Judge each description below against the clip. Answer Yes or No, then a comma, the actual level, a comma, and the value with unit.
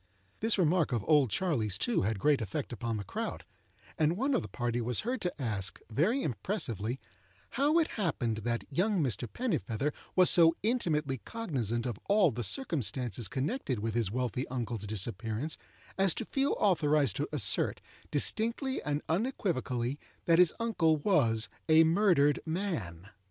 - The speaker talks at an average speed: Yes, average, 155 wpm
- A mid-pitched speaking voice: Yes, medium, 145 Hz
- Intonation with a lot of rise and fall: Yes, wide, 7.9 semitones